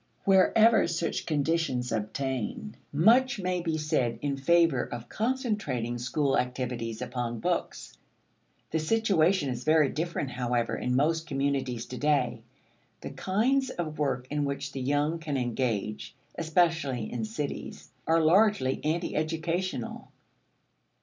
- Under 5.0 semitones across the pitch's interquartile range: No, average, 5.3 semitones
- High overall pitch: No, medium, 145 Hz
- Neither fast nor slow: No, slow, 125 wpm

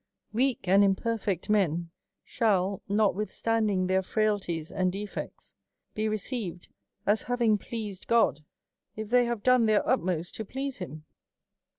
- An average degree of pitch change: Yes, average, 3.4 semitones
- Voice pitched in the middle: No, high, 210 Hz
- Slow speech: No, average, 155 wpm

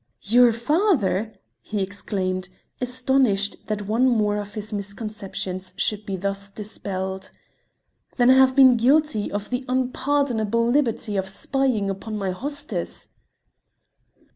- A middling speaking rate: No, slow, 120 wpm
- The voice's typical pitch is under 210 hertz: No, high, 215 Hz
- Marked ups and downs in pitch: No, average, 4.2 semitones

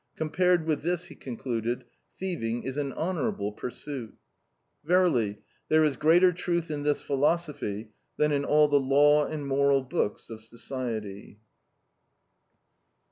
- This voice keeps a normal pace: No, slow, 130 wpm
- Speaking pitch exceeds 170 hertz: No, medium, 145 Hz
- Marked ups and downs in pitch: No, average, 4.6 semitones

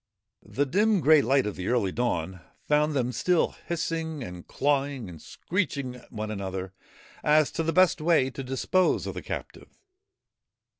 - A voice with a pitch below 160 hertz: Yes, low, 135 Hz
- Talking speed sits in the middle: Yes, average, 160 wpm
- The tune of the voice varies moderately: No, wide, 6.3 semitones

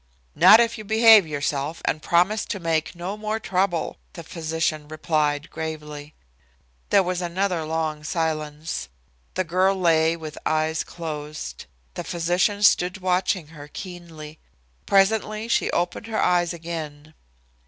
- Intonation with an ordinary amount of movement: Yes, average, 3.3 semitones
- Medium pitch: Yes, medium, 170 Hz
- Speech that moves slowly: Yes, slow, 130 wpm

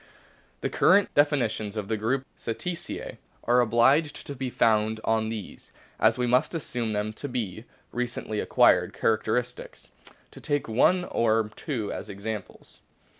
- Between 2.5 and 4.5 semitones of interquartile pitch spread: Yes, average, 3.2 semitones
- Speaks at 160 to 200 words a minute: No, average, 140 wpm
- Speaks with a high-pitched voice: No, low, 115 Hz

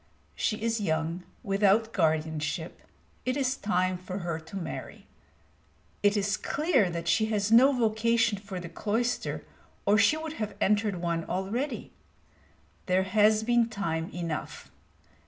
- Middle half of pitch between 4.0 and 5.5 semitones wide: Yes, average, 4.3 semitones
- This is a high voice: Yes, high, 205 Hz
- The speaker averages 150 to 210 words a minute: No, average, 140 wpm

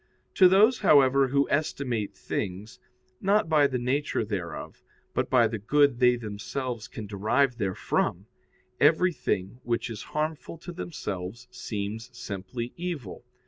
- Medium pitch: No, low, 125 Hz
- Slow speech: Yes, slow, 130 wpm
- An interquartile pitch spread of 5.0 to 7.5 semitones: Yes, wide, 5.5 semitones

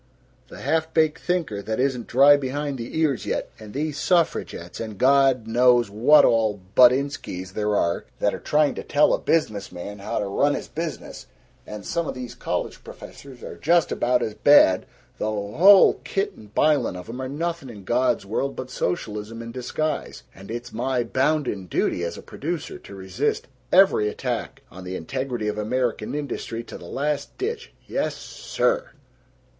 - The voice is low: Yes, low, 125 Hz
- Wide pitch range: Yes, wide, 5.8 semitones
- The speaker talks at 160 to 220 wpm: Yes, average, 175 wpm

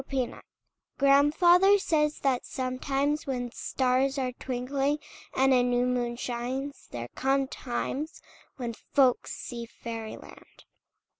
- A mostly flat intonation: Yes, narrow, 2.3 semitones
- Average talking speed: No, slow, 120 wpm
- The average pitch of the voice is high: Yes, very high, 260 Hz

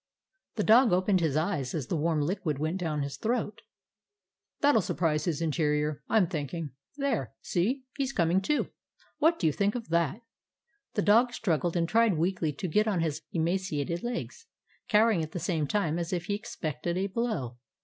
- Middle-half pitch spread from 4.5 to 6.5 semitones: Yes, average, 5.3 semitones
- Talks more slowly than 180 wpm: No, average, 190 wpm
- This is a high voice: No, medium, 175 Hz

